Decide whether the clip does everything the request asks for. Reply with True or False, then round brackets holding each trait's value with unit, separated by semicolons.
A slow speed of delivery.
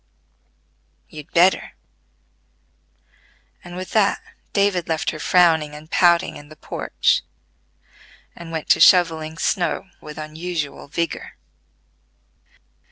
True (100 wpm)